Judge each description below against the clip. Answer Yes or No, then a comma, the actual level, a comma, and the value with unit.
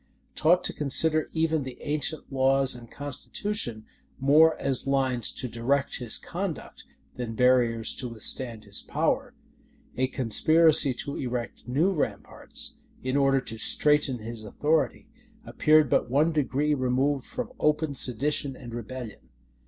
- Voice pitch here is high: No, low, 135 Hz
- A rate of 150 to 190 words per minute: No, slow, 135 wpm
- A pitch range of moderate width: Yes, average, 3.7 semitones